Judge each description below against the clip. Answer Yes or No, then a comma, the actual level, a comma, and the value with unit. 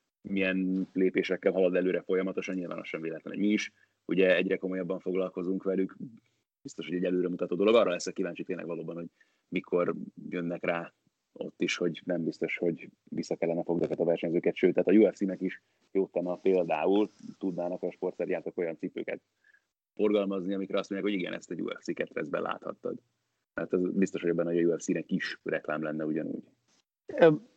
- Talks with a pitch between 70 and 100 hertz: Yes, very low, 95 Hz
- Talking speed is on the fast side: Yes, fast, 170 wpm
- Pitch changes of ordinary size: No, narrow, 1.8 semitones